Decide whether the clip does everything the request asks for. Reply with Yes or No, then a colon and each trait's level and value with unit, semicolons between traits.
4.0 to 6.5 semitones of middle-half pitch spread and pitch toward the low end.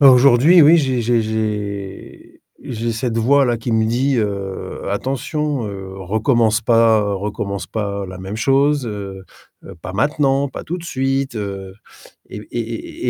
Yes: average, 4.8 semitones; low, 115 Hz